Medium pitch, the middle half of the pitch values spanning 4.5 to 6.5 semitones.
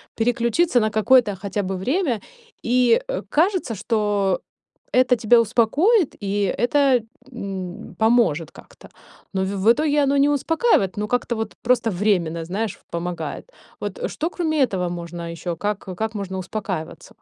No: high, 220 Hz; average, 5.2 semitones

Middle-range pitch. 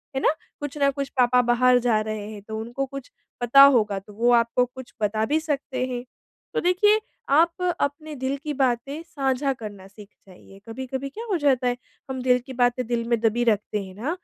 No: very high, 250 Hz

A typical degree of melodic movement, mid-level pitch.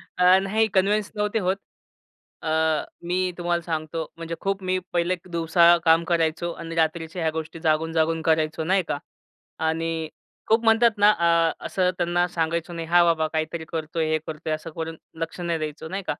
No: narrow, 1.9 semitones; medium, 165 Hz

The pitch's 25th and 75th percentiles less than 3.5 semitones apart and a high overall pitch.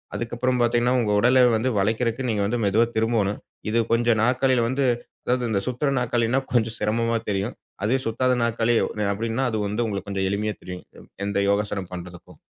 No: average, 2.9 semitones; low, 115 Hz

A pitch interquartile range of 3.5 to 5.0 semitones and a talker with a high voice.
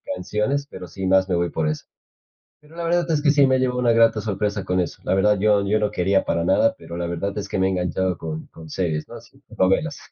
No: average, 4.2 semitones; very low, 95 Hz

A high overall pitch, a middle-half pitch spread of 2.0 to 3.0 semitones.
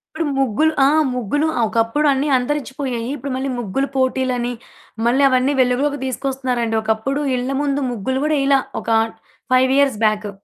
Yes: very high, 260 Hz; average, 2.7 semitones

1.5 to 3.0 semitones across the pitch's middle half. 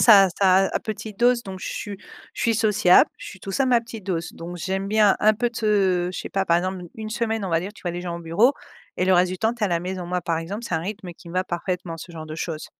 No: average, 3.6 semitones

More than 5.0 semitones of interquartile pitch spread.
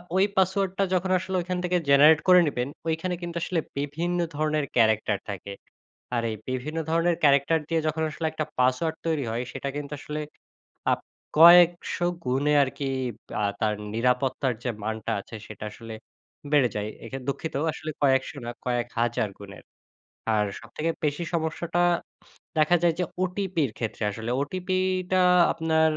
Yes: wide, 5.4 semitones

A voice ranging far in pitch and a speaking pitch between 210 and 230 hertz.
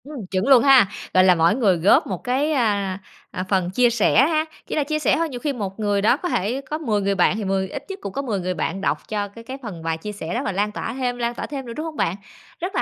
Yes: wide, 5.7 semitones; high, 220 Hz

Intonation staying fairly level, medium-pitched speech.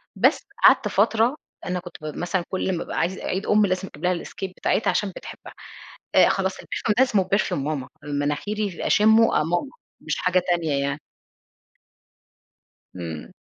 No: average, 5.1 semitones; medium, 180 Hz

